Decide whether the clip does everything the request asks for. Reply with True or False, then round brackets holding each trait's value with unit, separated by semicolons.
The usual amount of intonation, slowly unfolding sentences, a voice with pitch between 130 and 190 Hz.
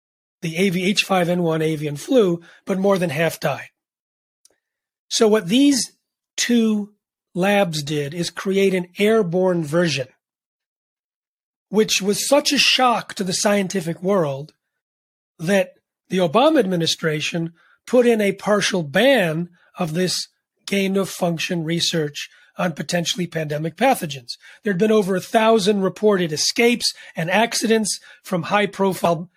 True (3.9 semitones; 120 wpm; 185 Hz)